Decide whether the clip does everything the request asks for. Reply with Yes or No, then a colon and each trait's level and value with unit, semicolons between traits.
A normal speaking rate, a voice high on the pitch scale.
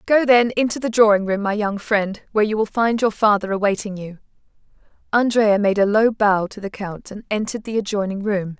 No: fast, 210 wpm; high, 210 Hz